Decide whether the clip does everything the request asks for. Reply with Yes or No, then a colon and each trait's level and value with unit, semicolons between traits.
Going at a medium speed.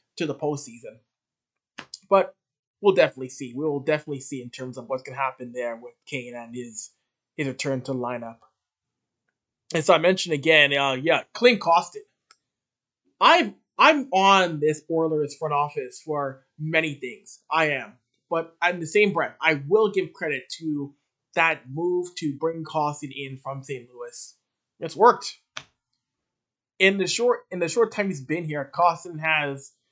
Yes: average, 165 wpm